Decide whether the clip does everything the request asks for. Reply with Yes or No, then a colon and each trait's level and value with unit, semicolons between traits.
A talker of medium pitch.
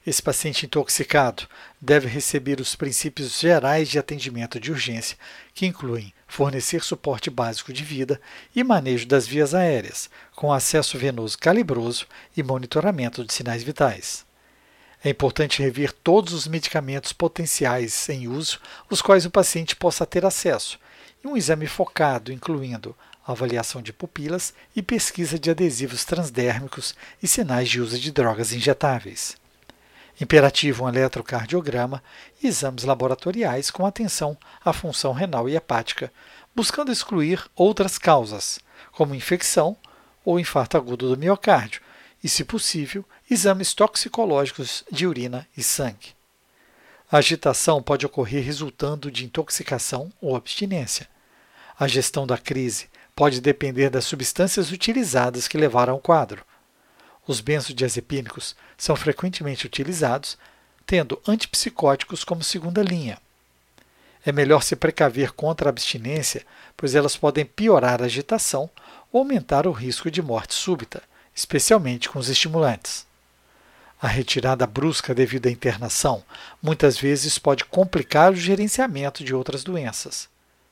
Yes: medium, 145 Hz